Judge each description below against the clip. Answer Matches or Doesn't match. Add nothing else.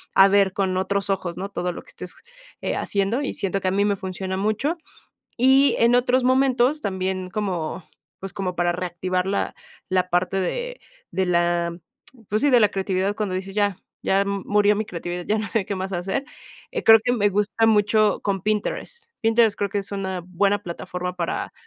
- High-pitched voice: Matches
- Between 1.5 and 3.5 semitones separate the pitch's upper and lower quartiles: Matches